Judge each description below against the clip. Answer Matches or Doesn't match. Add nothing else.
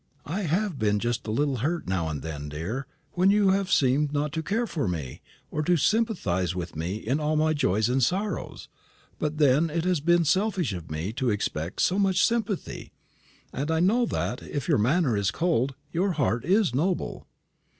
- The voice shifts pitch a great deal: Matches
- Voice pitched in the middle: Matches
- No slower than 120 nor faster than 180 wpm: Doesn't match